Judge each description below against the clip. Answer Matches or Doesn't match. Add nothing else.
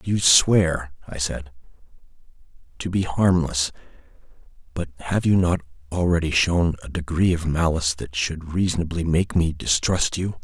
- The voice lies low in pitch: Matches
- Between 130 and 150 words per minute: Matches